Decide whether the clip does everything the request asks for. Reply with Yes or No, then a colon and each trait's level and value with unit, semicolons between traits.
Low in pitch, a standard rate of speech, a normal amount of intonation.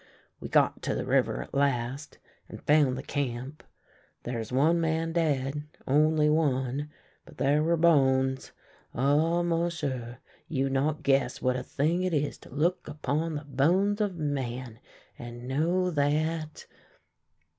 No: medium, 145 Hz; average, 150 wpm; average, 3.5 semitones